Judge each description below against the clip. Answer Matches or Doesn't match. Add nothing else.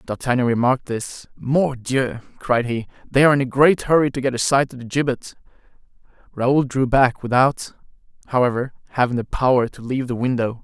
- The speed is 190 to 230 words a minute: Doesn't match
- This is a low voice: Matches